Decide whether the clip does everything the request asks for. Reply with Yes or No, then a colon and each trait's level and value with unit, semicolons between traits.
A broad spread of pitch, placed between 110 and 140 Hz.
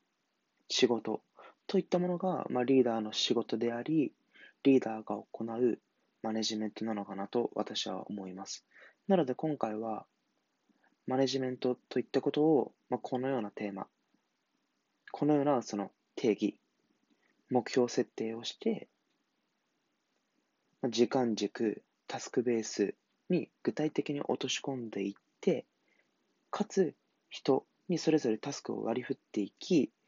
No: average, 4.5 semitones; low, 125 Hz